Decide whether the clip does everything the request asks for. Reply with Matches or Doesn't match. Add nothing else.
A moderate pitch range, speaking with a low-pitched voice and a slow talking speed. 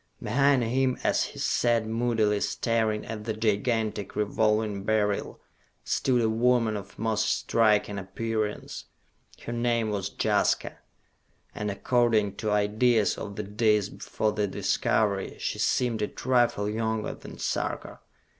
Doesn't match